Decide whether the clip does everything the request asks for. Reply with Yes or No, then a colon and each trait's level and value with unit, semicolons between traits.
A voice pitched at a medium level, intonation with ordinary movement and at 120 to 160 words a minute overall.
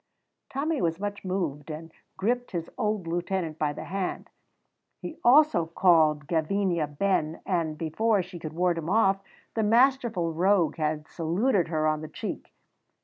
Yes: medium, 175 Hz; average, 4.3 semitones; average, 150 wpm